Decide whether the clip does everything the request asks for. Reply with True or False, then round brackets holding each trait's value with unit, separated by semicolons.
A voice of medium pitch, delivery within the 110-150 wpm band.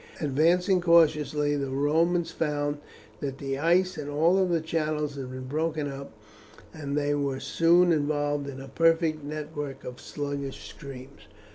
True (150 Hz; 145 wpm)